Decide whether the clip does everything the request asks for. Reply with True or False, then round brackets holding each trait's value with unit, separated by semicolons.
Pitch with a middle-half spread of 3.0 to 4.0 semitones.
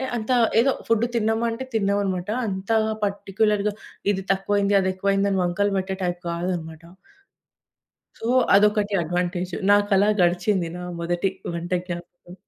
False (2.6 semitones)